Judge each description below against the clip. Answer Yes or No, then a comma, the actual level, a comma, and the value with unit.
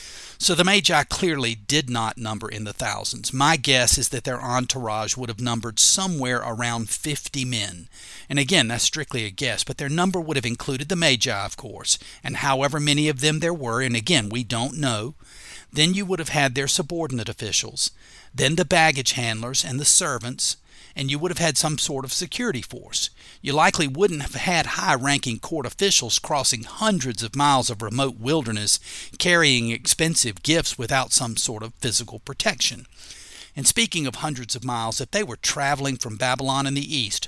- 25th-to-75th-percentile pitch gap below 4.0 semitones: No, average, 4.7 semitones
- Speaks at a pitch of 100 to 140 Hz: Yes, low, 135 Hz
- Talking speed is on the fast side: No, average, 185 wpm